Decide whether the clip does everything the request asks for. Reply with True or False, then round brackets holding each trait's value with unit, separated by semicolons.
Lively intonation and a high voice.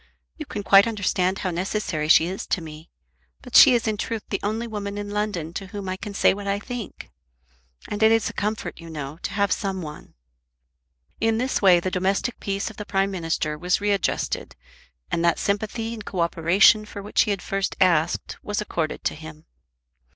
False (3.2 semitones; 195 Hz)